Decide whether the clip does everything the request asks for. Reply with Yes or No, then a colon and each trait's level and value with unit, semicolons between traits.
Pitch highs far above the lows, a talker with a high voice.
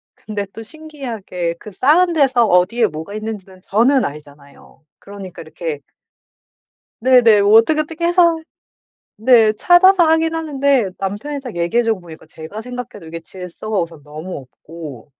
Yes: wide, 8.0 semitones; high, 215 Hz